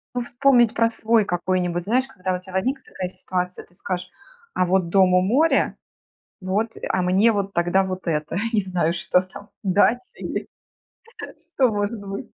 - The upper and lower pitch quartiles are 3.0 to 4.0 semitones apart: Yes, average, 3.6 semitones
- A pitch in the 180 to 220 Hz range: Yes, high, 190 Hz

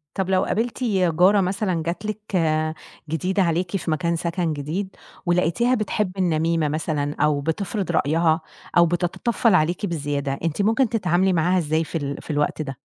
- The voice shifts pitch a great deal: No, average, 3.4 semitones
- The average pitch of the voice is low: No, medium, 175 Hz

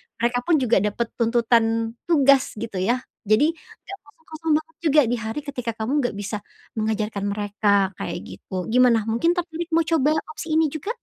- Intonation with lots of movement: Yes, wide, 6.1 semitones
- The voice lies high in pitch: Yes, high, 240 Hz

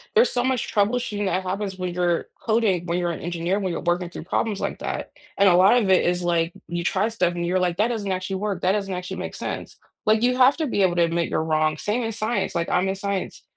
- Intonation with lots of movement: No, average, 3.3 semitones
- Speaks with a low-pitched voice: No, high, 190 Hz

